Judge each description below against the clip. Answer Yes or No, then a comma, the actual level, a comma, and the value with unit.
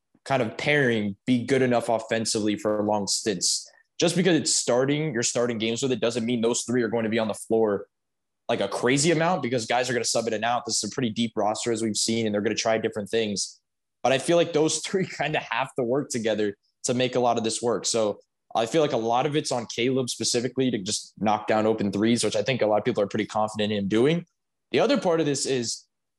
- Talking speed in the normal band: No, fast, 260 wpm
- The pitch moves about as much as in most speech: Yes, average, 3.2 semitones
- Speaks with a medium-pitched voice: No, low, 120 Hz